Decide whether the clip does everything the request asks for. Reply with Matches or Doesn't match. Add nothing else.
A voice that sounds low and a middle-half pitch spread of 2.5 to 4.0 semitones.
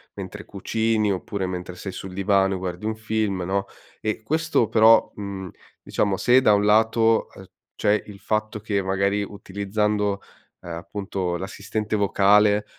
Doesn't match